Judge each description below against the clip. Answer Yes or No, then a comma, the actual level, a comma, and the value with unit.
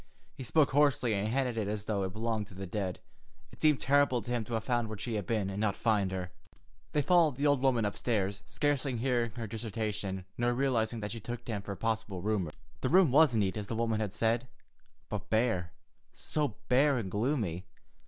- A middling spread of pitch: Yes, average, 3.7 semitones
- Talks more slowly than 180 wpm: No, fast, 205 wpm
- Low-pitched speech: Yes, low, 110 Hz